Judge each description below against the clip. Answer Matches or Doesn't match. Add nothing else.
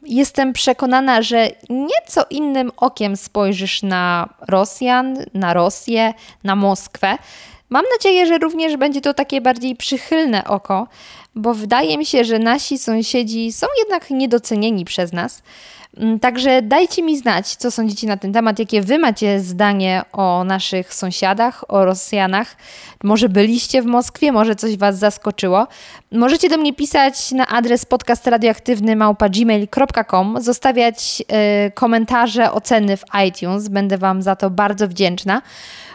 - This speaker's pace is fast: Doesn't match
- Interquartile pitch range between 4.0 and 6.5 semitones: Matches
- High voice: Matches